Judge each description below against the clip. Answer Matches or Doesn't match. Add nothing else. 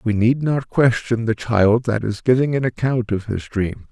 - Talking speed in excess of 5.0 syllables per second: Doesn't match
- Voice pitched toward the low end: Matches